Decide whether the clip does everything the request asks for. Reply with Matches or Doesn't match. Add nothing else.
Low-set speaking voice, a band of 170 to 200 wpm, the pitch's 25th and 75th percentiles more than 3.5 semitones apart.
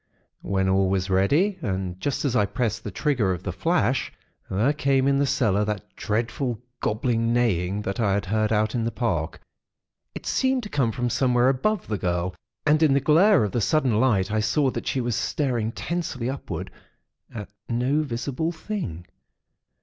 Matches